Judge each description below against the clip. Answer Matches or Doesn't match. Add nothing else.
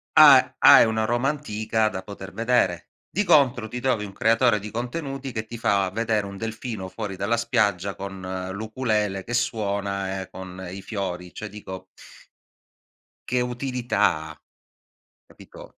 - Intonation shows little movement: Doesn't match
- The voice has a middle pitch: Doesn't match